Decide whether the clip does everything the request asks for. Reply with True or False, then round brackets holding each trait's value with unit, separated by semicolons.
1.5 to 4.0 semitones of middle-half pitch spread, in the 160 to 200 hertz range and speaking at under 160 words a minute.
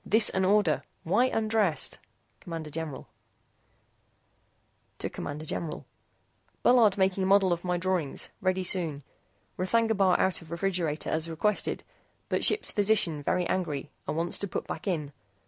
True (3.7 semitones; 185 Hz; 135 wpm)